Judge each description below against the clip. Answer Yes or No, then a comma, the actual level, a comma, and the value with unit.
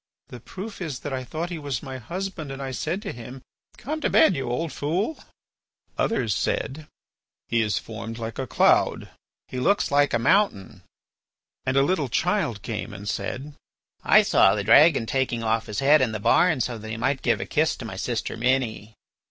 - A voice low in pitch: Yes, low, 130 Hz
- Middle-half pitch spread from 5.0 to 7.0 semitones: Yes, wide, 5.5 semitones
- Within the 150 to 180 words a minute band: No, average, 195 wpm